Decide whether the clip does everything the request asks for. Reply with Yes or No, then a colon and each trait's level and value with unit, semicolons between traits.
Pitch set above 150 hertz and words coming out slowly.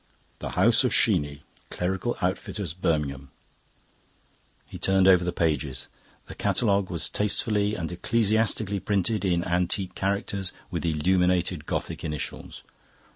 No: very low, 90 Hz; slow, 120 wpm